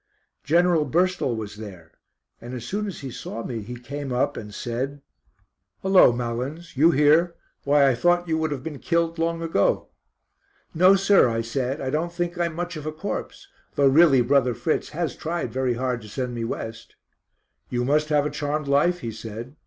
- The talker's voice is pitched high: No, medium, 140 Hz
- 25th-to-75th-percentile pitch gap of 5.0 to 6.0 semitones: Yes, wide, 5.4 semitones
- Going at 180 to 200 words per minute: Yes, average, 190 wpm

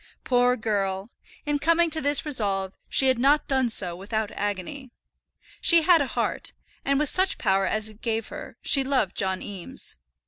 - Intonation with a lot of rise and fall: Yes, wide, 6.1 semitones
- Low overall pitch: No, high, 245 Hz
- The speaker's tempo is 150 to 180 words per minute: Yes, average, 175 wpm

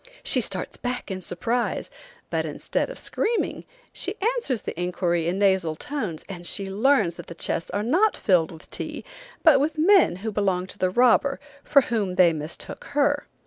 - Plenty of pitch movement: Yes, wide, 7.8 semitones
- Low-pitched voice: No, high, 205 Hz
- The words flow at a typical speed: Yes, average, 180 wpm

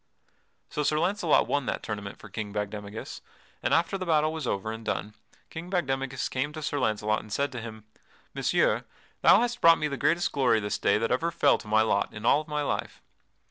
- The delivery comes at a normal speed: No, fast, 220 wpm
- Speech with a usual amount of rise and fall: No, wide, 6.2 semitones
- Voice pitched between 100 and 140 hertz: Yes, low, 135 Hz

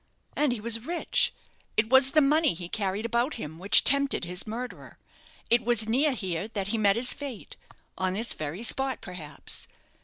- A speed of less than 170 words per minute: No, average, 180 wpm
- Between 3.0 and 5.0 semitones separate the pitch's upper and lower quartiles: No, wide, 5.5 semitones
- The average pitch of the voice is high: Yes, high, 225 Hz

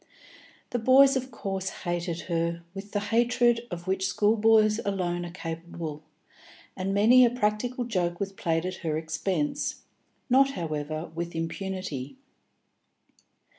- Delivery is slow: Yes, slow, 130 wpm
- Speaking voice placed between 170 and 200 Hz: Yes, high, 190 Hz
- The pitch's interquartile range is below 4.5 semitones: No, average, 4.9 semitones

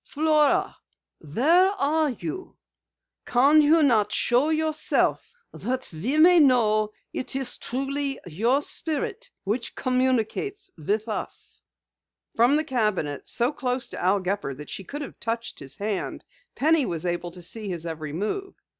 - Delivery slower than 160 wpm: Yes, average, 145 wpm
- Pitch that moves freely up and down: Yes, wide, 7.0 semitones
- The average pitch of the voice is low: No, very high, 250 Hz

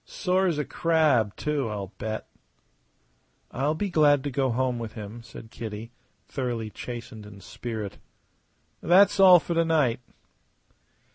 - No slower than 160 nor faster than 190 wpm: No, average, 140 wpm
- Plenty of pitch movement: Yes, wide, 6.2 semitones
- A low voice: Yes, low, 125 Hz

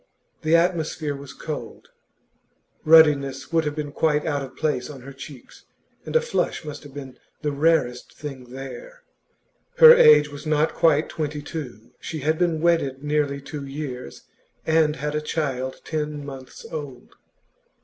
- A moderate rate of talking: Yes, average, 160 wpm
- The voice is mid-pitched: Yes, medium, 150 Hz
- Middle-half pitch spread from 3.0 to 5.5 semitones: No, narrow, 2.4 semitones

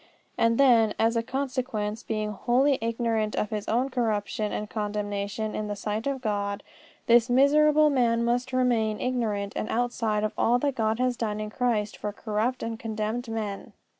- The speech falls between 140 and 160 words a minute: No, average, 170 wpm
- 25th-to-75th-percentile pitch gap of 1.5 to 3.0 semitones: Yes, average, 2.7 semitones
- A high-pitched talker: Yes, high, 225 Hz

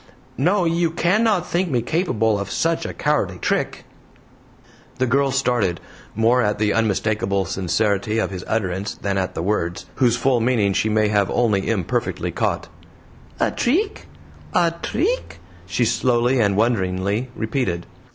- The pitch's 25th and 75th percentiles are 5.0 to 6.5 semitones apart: Yes, wide, 5.5 semitones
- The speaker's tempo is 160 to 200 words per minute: No, average, 145 wpm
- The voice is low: Yes, low, 115 Hz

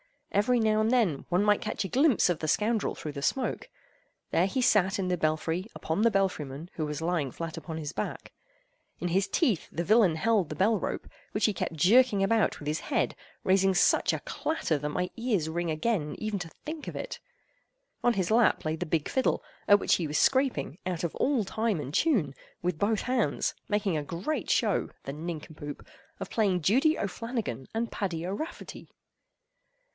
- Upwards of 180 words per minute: Yes, average, 195 wpm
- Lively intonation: Yes, wide, 5.7 semitones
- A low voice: No, high, 190 Hz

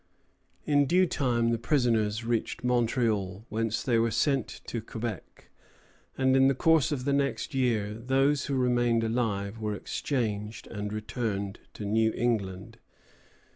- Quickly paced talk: No, average, 145 wpm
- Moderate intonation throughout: Yes, average, 3.6 semitones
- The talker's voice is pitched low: Yes, low, 115 Hz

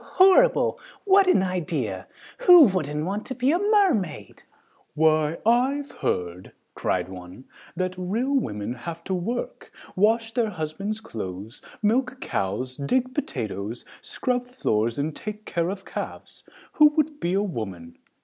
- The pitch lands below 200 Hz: Yes, medium, 185 Hz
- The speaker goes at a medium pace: No, slow, 130 wpm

